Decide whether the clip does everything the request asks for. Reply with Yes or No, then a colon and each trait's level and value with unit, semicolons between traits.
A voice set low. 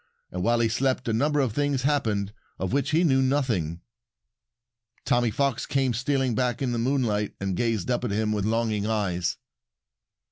Yes: low, 120 Hz